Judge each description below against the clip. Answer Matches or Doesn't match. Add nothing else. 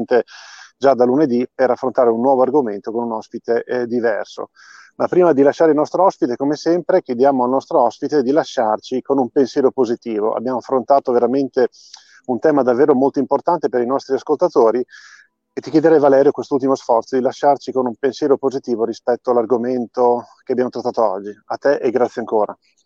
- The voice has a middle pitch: Doesn't match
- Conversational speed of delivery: Doesn't match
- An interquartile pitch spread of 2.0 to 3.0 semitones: Matches